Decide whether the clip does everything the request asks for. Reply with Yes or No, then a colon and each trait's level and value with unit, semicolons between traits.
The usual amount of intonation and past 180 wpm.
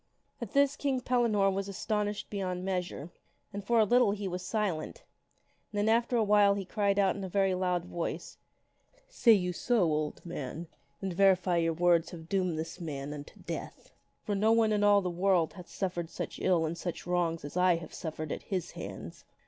Yes: average, 3.4 semitones; fast, 205 wpm